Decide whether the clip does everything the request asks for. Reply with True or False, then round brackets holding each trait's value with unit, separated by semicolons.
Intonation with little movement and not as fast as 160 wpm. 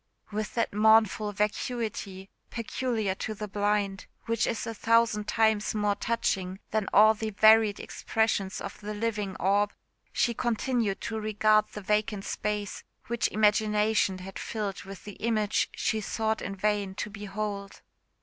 True (1.4 semitones; 145 wpm)